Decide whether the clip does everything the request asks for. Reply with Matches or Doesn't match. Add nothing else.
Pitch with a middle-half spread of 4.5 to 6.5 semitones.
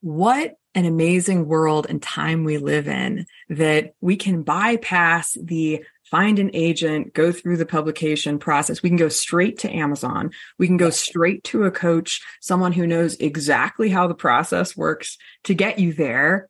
Doesn't match